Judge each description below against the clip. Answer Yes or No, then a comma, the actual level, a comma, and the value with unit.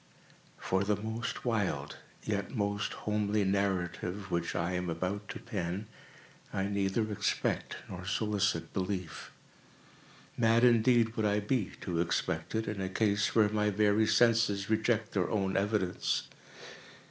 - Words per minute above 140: No, slow, 135 wpm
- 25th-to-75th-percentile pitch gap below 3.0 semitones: Yes, narrow, 2.5 semitones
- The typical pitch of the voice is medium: No, low, 100 Hz